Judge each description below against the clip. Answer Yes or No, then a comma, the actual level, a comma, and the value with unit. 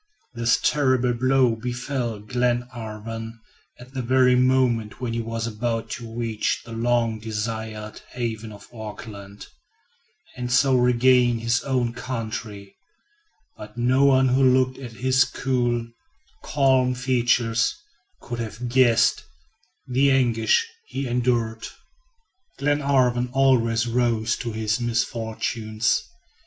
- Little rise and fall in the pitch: Yes, narrow, 2.1 semitones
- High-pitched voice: No, low, 120 Hz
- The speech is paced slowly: Yes, slow, 115 wpm